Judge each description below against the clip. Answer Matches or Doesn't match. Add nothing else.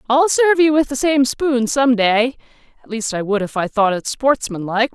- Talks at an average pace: Doesn't match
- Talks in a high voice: Matches